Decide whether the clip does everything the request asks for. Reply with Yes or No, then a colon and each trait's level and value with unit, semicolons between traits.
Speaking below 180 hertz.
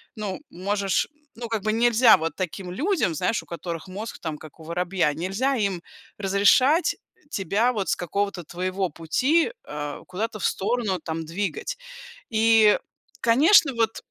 No: high, 200 Hz